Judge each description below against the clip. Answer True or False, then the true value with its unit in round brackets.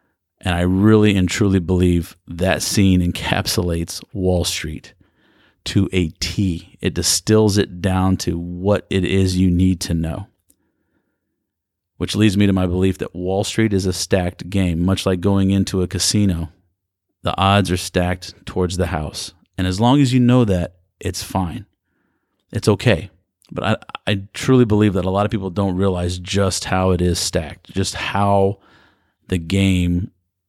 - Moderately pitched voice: False (95 Hz)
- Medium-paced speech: True (165 wpm)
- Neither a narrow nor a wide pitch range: False (1.9 semitones)